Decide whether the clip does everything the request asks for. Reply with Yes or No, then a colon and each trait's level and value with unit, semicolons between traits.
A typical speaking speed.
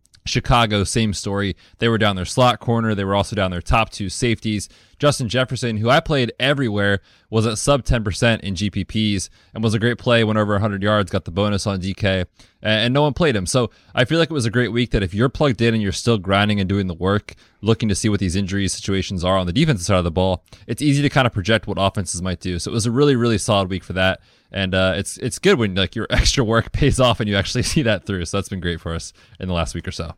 No: fast, 270 wpm